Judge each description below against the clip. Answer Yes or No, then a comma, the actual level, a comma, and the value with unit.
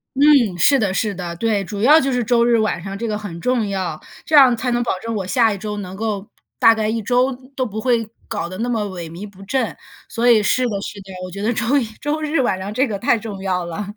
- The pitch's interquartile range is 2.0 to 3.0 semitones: No, average, 3.8 semitones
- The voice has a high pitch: Yes, high, 215 Hz